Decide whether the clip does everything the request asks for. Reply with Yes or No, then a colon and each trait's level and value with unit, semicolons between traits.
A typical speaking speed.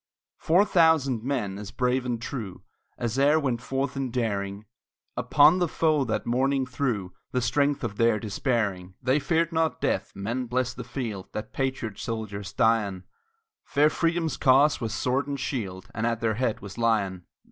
Yes: average, 170 wpm